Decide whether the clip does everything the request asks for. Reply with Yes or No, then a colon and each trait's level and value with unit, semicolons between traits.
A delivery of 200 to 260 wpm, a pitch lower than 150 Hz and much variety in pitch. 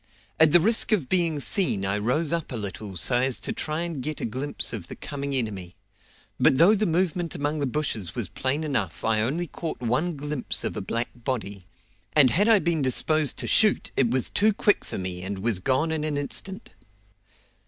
Yes: fast, 205 wpm; medium, 140 Hz; wide, 6.3 semitones